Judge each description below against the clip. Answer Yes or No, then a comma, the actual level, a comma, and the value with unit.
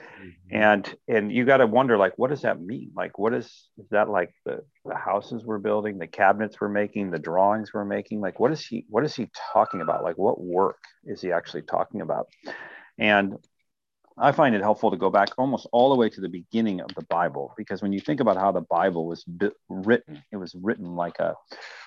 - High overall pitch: No, low, 100 Hz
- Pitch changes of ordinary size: No, narrow, 2.2 semitones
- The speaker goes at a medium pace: No, fast, 220 wpm